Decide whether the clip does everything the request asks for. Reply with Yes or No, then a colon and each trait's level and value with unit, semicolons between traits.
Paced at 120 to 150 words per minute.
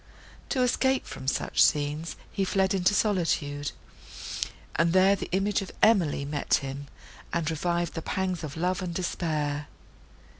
Yes: average, 145 wpm